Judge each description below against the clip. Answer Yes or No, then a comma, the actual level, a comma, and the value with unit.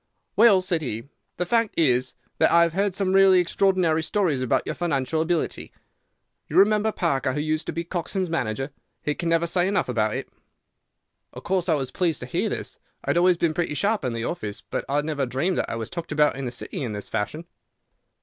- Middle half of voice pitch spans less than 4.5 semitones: No, average, 5.3 semitones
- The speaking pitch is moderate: Yes, medium, 165 Hz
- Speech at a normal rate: No, fast, 220 wpm